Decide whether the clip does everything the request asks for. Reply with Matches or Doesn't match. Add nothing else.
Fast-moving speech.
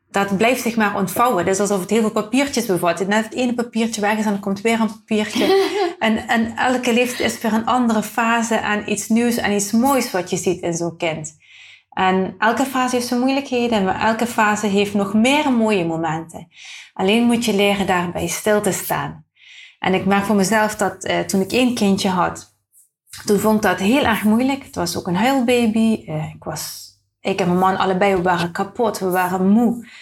Matches